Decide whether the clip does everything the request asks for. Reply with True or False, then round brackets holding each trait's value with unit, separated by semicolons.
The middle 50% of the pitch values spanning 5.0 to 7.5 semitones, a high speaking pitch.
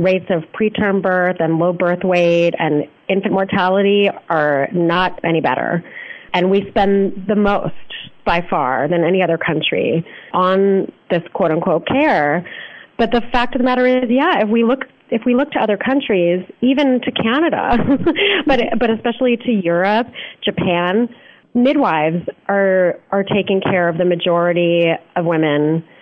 True (5.3 semitones; 195 Hz)